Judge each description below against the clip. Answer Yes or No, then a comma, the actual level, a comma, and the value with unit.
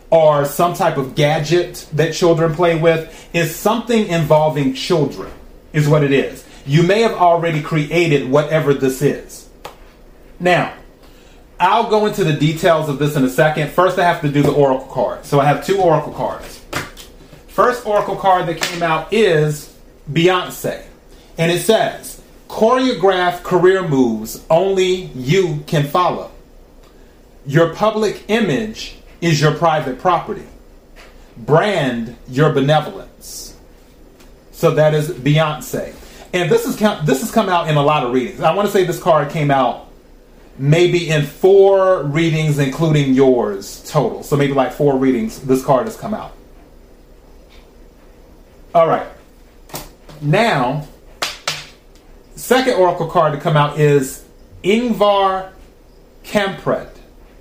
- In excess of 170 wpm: No, slow, 135 wpm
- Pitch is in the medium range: Yes, medium, 160 Hz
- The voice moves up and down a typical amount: Yes, average, 4.2 semitones